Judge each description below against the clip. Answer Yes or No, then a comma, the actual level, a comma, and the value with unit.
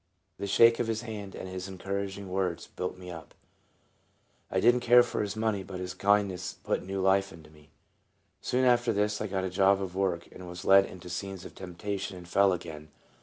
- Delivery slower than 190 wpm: No, fast, 205 wpm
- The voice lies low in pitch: Yes, very low, 95 Hz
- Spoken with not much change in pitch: Yes, narrow, 2.0 semitones